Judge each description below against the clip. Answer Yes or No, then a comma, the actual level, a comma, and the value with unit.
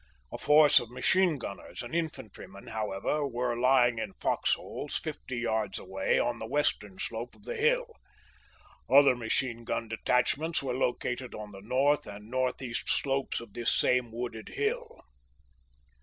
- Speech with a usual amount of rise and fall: Yes, average, 3.5 semitones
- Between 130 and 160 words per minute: Yes, average, 155 wpm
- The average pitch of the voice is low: Yes, low, 125 Hz